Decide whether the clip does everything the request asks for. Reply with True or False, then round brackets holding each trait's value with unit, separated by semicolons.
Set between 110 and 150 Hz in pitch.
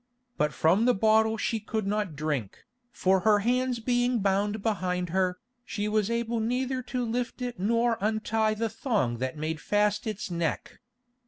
False (215 Hz)